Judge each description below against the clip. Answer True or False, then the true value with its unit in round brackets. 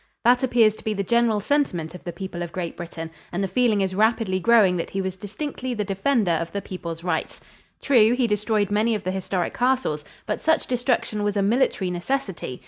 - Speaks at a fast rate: True (210 wpm)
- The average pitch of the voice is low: False (205 Hz)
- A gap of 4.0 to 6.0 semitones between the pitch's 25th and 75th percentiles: True (4.4 semitones)